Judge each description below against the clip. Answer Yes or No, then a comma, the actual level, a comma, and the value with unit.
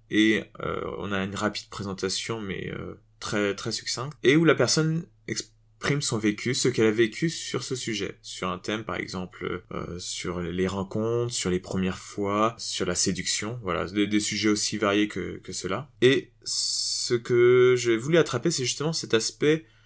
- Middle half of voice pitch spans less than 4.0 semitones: Yes, average, 3.6 semitones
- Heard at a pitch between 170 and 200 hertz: No, low, 110 Hz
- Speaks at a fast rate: No, average, 185 wpm